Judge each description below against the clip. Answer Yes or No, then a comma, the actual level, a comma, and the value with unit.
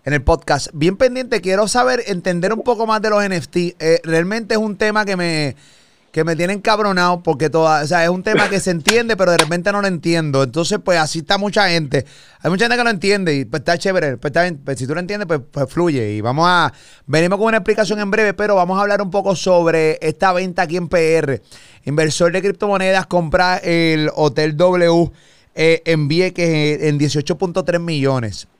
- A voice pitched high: No, medium, 175 Hz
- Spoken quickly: Yes, fast, 210 wpm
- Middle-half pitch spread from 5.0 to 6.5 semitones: No, average, 4.0 semitones